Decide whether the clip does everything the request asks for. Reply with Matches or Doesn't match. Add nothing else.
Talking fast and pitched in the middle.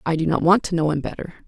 Matches